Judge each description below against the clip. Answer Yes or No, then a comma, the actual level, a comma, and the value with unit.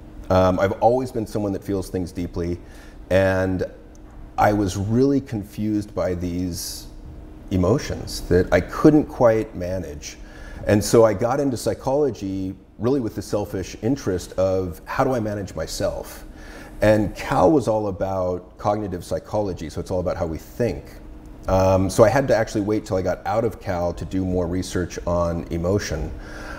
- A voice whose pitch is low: Yes, very low, 95 Hz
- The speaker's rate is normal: Yes, average, 165 wpm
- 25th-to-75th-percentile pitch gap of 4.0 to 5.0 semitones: No, average, 3.3 semitones